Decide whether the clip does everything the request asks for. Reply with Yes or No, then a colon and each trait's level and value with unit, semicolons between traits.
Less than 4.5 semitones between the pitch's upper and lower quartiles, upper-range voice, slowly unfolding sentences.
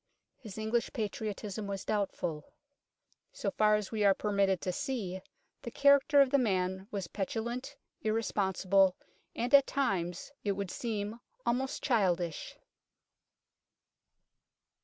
Yes: average, 3.9 semitones; high, 210 Hz; slow, 115 wpm